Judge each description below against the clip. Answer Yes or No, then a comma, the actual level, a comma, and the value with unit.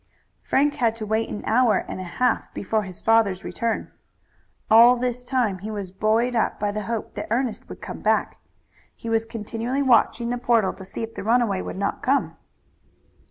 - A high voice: Yes, high, 225 Hz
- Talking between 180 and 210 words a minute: Yes, average, 190 wpm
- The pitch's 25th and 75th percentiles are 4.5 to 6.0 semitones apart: No, average, 2.7 semitones